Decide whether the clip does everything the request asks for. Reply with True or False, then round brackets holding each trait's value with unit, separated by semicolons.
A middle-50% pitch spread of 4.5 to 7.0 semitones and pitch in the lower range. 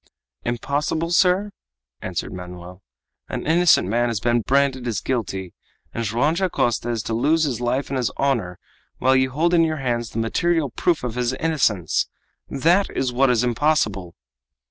True (5.4 semitones; 125 Hz)